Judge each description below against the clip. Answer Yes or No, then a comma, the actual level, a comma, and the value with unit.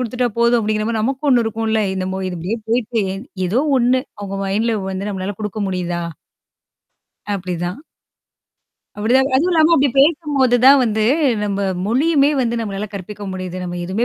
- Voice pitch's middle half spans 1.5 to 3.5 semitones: No, average, 4.6 semitones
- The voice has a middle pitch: No, high, 220 Hz